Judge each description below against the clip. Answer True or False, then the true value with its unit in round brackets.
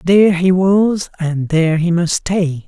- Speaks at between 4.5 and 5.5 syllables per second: False (4.1 syllables/s)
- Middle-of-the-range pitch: True (175 Hz)